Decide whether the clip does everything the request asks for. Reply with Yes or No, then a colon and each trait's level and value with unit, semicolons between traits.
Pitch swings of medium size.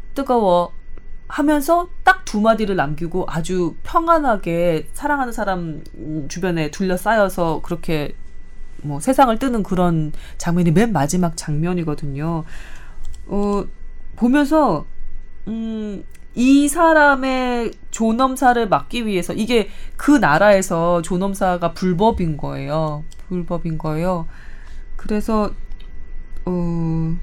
No: wide, 5.8 semitones